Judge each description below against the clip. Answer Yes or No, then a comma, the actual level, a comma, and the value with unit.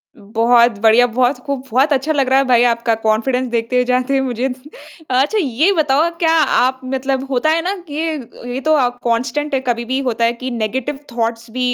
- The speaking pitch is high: Yes, very high, 255 Hz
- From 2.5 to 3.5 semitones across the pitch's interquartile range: Yes, average, 2.9 semitones